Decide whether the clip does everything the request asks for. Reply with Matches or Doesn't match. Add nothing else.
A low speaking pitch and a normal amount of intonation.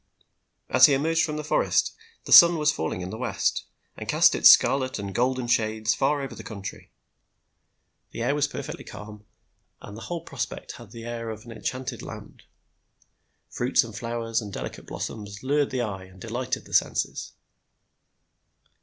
Matches